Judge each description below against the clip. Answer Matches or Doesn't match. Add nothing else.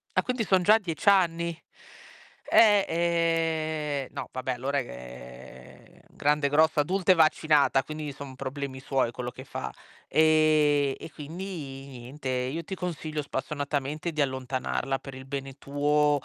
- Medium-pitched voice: Matches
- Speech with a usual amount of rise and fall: Matches